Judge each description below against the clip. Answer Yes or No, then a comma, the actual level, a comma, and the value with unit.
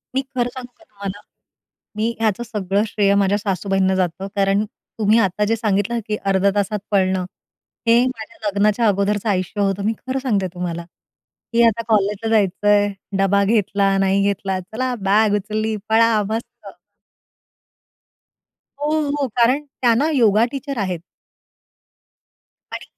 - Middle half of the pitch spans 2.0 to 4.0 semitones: Yes, average, 2.7 semitones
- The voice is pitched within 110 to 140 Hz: No, high, 210 Hz